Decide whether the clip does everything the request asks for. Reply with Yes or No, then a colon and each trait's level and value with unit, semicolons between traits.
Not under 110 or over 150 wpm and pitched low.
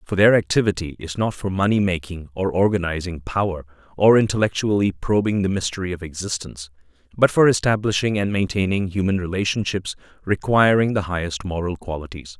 Yes: average, 145 wpm; very low, 95 Hz